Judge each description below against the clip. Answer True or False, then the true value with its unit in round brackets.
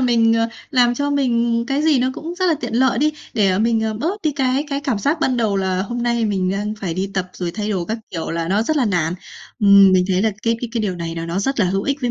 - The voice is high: True (225 Hz)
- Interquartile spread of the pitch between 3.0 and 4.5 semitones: False (5.1 semitones)